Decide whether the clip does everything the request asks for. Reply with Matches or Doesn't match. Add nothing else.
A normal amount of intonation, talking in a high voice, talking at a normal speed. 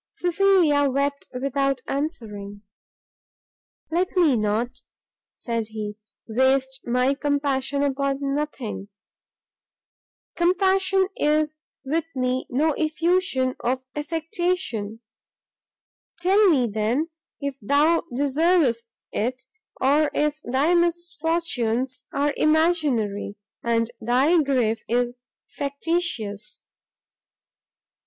Doesn't match